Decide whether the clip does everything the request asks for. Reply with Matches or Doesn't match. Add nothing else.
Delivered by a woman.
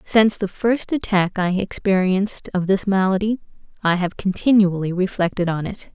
Matches